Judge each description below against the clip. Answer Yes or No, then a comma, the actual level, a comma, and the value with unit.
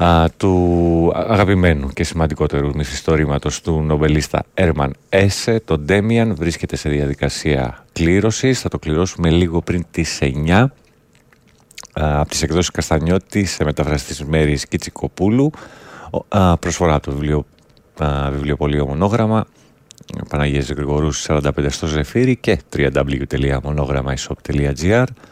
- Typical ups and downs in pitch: Yes, average, 4.1 semitones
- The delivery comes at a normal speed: No, slow, 110 wpm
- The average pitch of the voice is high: No, very low, 80 Hz